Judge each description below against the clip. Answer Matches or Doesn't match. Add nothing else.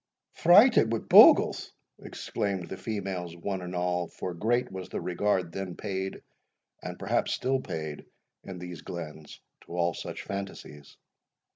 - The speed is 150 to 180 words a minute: Doesn't match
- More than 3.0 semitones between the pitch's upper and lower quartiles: Doesn't match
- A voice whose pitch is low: Matches